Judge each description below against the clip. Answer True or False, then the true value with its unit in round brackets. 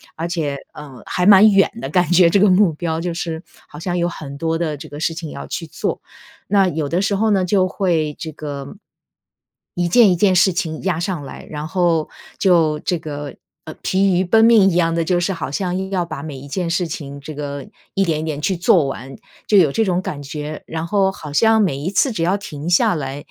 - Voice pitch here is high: False (170 Hz)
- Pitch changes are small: False (3.8 semitones)